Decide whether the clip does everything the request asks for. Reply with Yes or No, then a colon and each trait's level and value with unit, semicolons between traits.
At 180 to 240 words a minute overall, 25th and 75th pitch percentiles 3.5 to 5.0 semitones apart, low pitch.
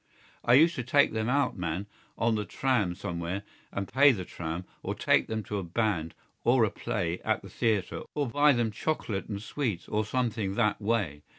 Yes: average, 195 wpm; average, 4.2 semitones; low, 110 Hz